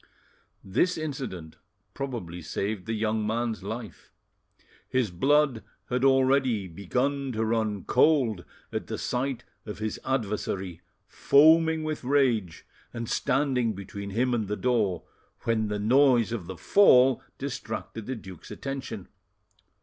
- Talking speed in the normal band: No, slow, 125 wpm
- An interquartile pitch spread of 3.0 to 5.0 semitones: Yes, average, 4.5 semitones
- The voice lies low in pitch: Yes, low, 115 Hz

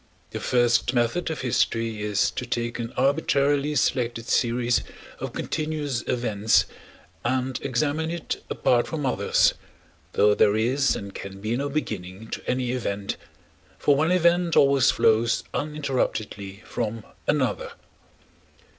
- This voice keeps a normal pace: No, slow, 130 wpm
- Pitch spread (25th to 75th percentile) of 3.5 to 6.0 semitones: Yes, average, 4.2 semitones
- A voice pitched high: No, low, 125 Hz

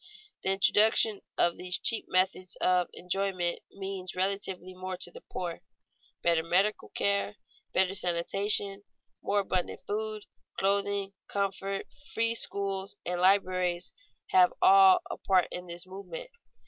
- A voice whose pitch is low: No, high, 195 Hz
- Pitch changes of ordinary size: No, narrow, 1.7 semitones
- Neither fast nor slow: No, slow, 125 wpm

